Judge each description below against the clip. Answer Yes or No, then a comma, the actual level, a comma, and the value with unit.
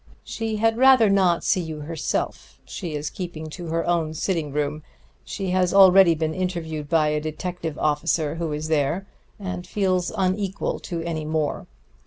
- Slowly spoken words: No, average, 165 wpm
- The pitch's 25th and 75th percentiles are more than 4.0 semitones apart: No, average, 3.1 semitones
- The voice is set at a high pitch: No, medium, 170 Hz